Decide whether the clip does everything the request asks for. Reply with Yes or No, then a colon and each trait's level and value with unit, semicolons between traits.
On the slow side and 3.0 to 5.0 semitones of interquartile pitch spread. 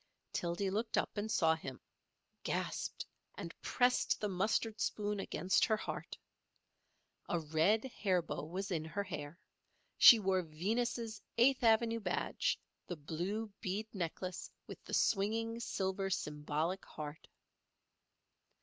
Yes: slow, 125 wpm; average, 4.5 semitones